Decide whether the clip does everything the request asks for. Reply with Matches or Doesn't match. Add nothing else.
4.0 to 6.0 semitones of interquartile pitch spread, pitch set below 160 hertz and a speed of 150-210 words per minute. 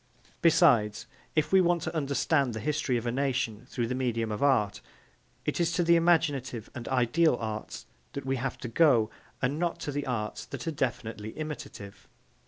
Matches